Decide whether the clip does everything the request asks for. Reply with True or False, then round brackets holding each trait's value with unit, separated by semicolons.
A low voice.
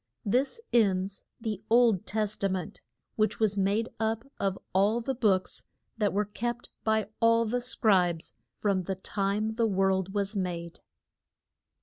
False (205 Hz)